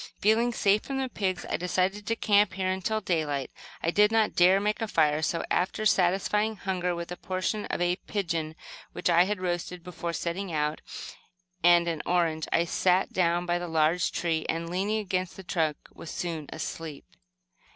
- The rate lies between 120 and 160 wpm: No, average, 180 wpm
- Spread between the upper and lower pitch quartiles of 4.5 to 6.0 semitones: No, average, 2.9 semitones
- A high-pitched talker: No, medium, 180 Hz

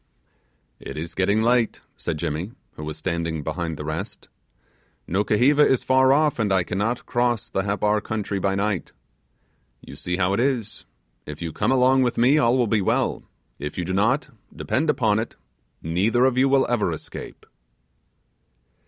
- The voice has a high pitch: No, low, 105 Hz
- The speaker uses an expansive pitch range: Yes, wide, 5.9 semitones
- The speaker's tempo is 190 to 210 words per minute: No, average, 170 wpm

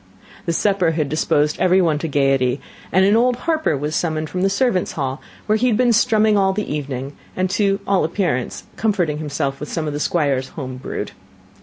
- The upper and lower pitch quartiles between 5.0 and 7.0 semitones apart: Yes, wide, 5.4 semitones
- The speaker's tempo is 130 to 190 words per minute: No, average, 200 wpm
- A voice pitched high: No, medium, 165 Hz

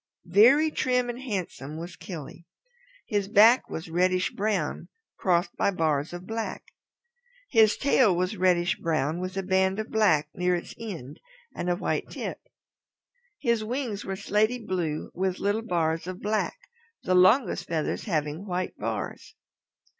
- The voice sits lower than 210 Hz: Yes, medium, 185 Hz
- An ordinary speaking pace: Yes, average, 145 wpm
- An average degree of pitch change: Yes, average, 3.9 semitones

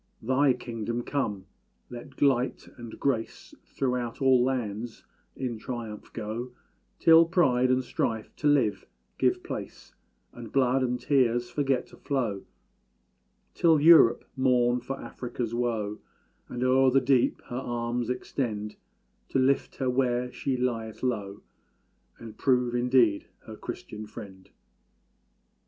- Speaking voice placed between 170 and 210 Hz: No, low, 125 Hz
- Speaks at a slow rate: Yes, slow, 125 wpm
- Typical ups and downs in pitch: No, narrow, 2.2 semitones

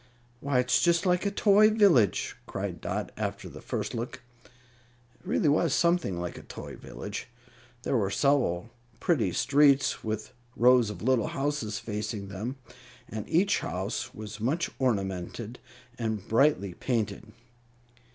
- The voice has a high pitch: No, low, 120 Hz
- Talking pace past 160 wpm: No, average, 140 wpm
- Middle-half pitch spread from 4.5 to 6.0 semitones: Yes, wide, 5.5 semitones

